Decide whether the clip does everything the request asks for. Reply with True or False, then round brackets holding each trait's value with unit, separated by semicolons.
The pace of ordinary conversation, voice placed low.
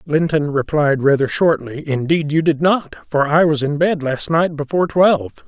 False (185 wpm; 150 Hz)